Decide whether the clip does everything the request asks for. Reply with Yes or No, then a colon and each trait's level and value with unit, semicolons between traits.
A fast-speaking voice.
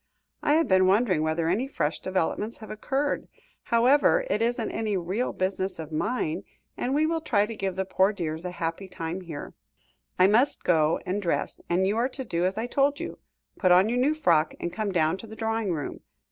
Yes: fast, 210 wpm